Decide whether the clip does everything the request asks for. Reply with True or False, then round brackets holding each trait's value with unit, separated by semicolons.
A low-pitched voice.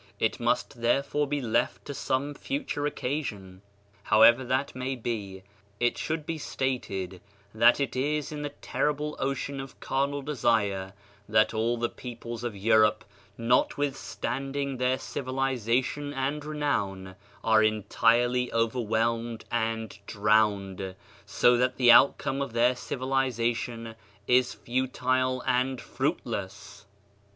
True (125 Hz)